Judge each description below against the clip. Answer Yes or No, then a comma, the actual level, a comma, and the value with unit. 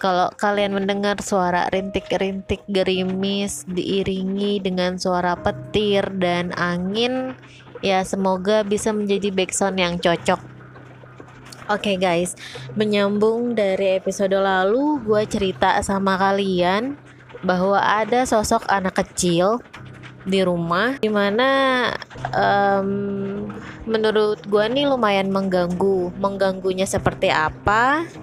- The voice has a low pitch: No, high, 195 Hz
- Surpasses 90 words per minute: Yes, average, 100 wpm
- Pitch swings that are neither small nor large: No, narrow, 1.9 semitones